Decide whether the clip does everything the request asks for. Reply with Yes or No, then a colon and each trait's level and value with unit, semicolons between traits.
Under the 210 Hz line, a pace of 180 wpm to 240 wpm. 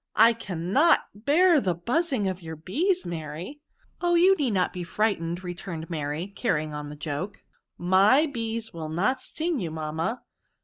Yes: high, 190 Hz; average, 185 wpm